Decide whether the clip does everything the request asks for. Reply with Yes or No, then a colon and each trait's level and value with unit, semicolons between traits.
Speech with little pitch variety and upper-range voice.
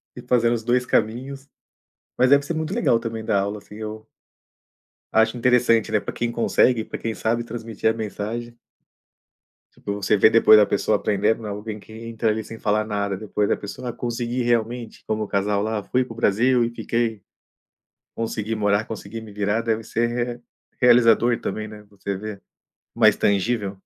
No: narrow, 2.1 semitones; low, 110 Hz